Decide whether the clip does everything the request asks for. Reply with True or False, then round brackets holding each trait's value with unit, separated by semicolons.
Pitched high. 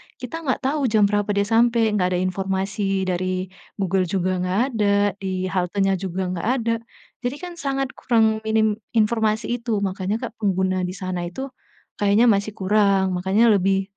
True (200 Hz)